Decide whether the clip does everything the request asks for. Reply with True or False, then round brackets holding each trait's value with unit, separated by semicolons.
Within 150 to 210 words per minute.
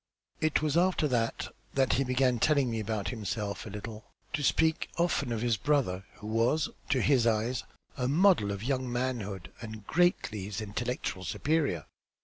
True (165 wpm)